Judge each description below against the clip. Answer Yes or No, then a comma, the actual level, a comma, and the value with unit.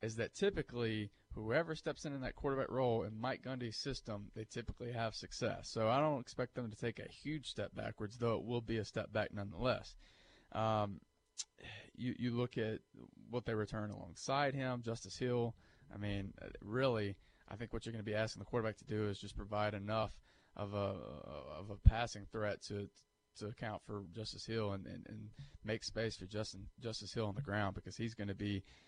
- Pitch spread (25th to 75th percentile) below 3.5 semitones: Yes, average, 2.9 semitones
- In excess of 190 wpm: Yes, average, 200 wpm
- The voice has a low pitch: Yes, low, 110 Hz